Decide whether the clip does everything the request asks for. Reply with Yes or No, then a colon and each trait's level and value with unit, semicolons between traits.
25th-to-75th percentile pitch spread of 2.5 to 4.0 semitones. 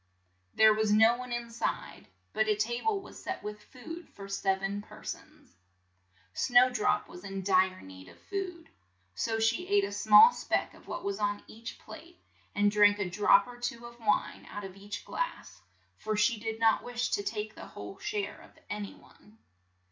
Yes: average, 3.1 semitones